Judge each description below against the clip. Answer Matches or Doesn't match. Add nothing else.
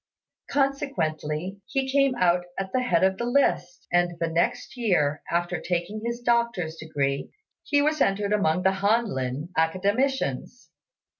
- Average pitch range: Doesn't match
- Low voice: Doesn't match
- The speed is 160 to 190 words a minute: Doesn't match